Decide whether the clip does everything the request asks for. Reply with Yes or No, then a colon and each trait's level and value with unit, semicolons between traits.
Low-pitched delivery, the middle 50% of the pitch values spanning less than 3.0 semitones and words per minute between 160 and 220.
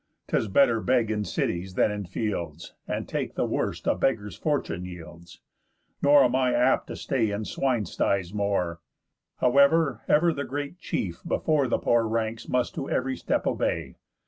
No: low, 115 Hz; average, 5.3 semitones; average, 170 wpm